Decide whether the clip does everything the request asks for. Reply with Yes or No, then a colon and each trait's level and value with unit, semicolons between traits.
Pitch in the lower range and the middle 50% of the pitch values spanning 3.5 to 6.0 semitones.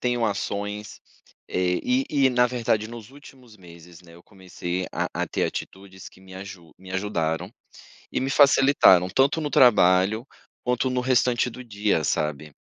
Yes: low, 105 Hz; average, 5.3 semitones